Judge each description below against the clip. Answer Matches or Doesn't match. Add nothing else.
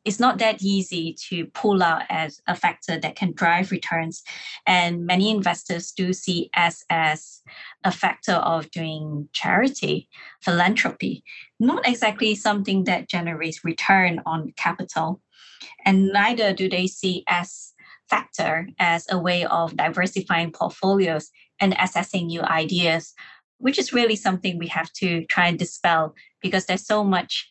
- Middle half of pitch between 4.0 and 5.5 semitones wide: Doesn't match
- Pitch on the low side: Doesn't match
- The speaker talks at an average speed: Matches